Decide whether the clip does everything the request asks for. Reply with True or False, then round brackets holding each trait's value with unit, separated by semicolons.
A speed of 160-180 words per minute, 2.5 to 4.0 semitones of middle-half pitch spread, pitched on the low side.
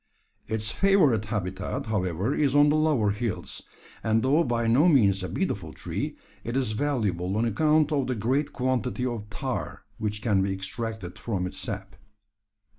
False (165 wpm; 5.0 semitones; 115 Hz)